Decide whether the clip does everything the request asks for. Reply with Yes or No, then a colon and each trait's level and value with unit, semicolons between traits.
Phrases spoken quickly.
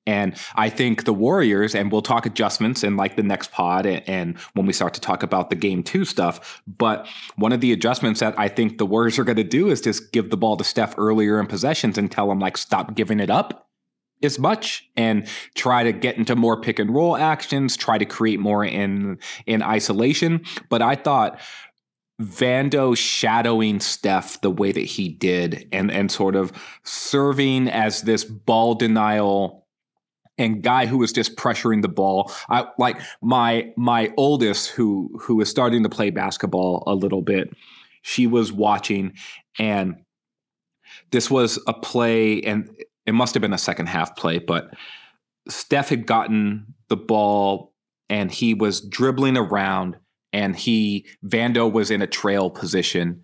No: average, 175 wpm